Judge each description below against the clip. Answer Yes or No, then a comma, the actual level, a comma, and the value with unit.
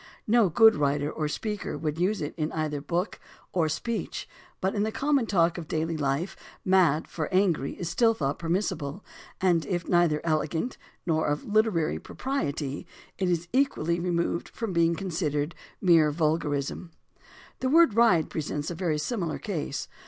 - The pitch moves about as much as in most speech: Yes, average, 4.4 semitones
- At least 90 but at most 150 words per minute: No, average, 160 wpm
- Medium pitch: Yes, medium, 170 Hz